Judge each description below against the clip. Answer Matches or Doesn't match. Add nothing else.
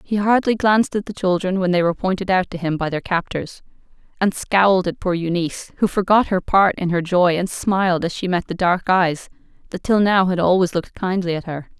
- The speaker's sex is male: Doesn't match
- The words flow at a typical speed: Doesn't match